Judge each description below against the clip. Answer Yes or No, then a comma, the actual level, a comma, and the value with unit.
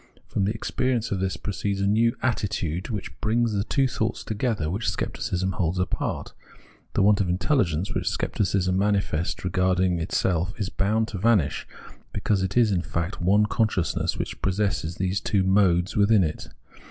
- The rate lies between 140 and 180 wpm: Yes, average, 165 wpm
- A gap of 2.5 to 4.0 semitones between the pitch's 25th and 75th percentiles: Yes, average, 2.8 semitones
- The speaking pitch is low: Yes, very low, 95 Hz